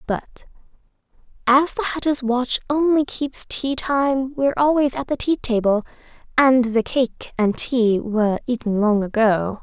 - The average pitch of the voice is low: No, very high, 250 Hz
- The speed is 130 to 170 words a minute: Yes, average, 150 wpm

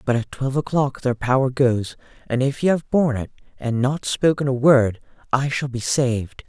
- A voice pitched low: Yes, low, 130 Hz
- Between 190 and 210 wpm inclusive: Yes, fast, 205 wpm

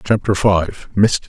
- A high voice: No, low, 100 Hz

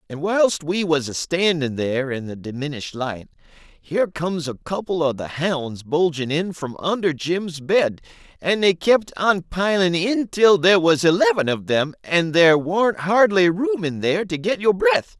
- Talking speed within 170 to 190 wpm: Yes, average, 185 wpm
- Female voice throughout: No, male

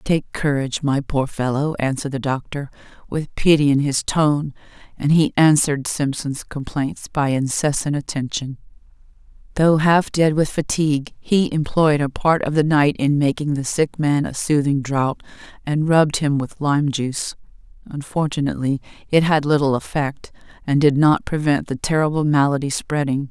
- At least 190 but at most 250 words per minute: No, average, 155 wpm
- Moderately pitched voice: Yes, medium, 145 Hz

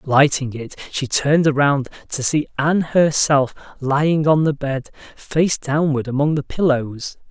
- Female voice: No, male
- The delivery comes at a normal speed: Yes, average, 150 wpm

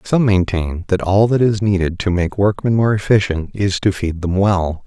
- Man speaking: Yes, male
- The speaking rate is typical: No, fast, 210 wpm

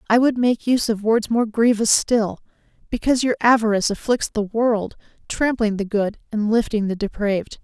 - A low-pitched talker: No, high, 220 Hz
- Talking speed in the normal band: Yes, average, 175 wpm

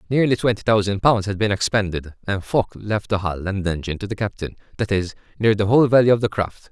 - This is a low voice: Yes, low, 100 Hz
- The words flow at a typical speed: No, fast, 230 wpm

